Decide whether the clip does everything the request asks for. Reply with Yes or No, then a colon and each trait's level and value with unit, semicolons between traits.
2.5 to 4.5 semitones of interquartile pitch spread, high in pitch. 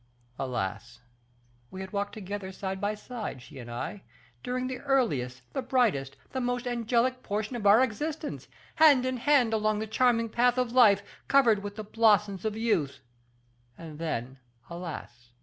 No: average, 5.2 semitones; high, 215 Hz